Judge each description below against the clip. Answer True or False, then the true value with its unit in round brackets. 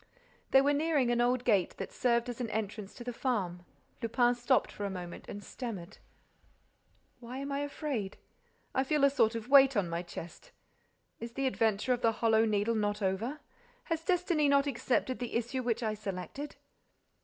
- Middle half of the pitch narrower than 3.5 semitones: False (4.3 semitones)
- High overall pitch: True (240 Hz)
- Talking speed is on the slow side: False (180 wpm)